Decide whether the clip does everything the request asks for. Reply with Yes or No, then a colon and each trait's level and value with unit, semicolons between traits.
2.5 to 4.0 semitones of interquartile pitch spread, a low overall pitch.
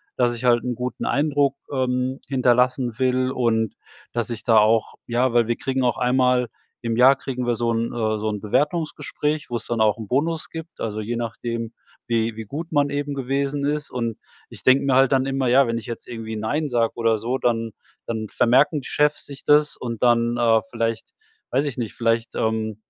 Yes: average, 2.8 semitones; low, 120 Hz